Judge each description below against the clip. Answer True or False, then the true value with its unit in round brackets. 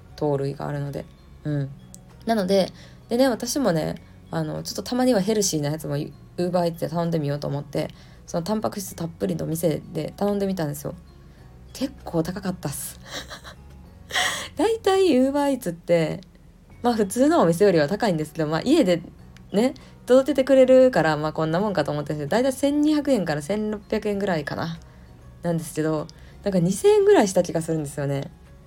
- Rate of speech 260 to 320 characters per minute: False (330 characters per minute)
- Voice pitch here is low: False (170 Hz)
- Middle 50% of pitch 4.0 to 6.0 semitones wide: False (6.9 semitones)